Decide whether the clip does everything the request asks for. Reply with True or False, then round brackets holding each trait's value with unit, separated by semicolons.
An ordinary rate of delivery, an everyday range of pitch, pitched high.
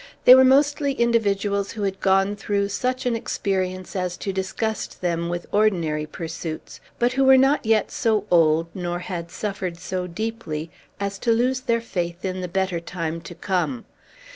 True (170 wpm; 4.6 semitones; 195 Hz)